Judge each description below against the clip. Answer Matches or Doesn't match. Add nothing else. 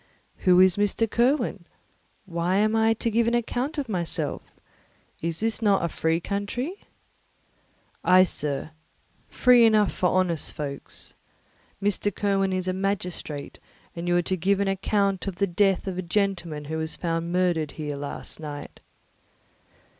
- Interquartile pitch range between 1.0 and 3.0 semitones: Doesn't match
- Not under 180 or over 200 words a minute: Doesn't match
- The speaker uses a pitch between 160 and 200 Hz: Matches